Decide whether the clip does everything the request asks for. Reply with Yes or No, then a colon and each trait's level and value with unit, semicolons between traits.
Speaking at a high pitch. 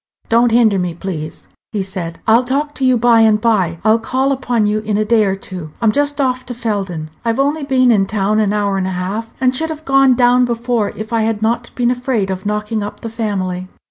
Yes: high, 225 Hz